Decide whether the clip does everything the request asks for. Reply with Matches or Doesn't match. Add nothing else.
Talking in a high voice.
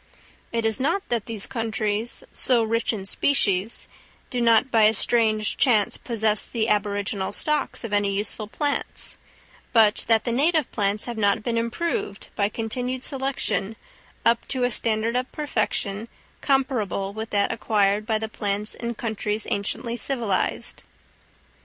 Matches